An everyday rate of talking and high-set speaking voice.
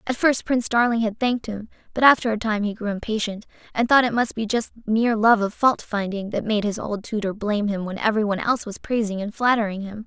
No: fast, 240 wpm; high, 220 Hz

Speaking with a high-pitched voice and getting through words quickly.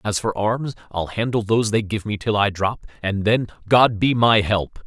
No: low, 105 Hz; fast, 220 wpm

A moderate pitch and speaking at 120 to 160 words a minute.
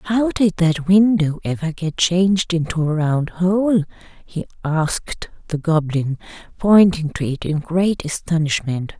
Yes: medium, 170 Hz; average, 140 wpm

